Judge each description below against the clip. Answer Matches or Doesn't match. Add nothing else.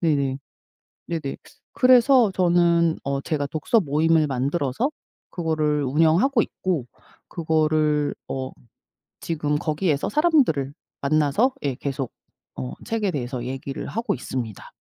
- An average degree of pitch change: Matches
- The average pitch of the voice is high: Doesn't match